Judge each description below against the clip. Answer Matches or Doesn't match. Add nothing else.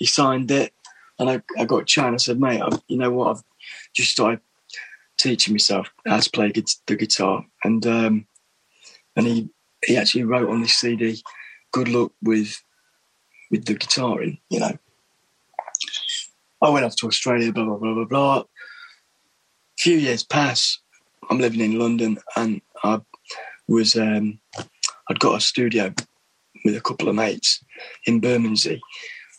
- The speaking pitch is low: Matches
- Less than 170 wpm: Matches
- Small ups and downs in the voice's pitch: Matches